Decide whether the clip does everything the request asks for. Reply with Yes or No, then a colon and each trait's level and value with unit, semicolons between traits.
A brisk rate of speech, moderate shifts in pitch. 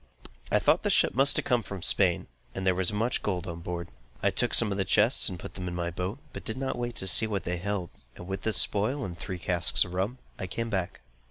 Yes: fast, 260 wpm; average, 3.7 semitones